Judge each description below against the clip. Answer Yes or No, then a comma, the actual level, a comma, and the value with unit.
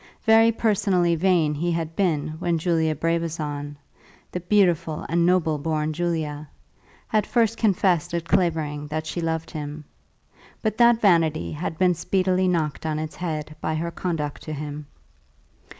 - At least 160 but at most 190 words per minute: No, average, 150 wpm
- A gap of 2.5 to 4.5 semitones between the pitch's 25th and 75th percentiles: Yes, average, 2.8 semitones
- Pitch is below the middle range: No, medium, 165 Hz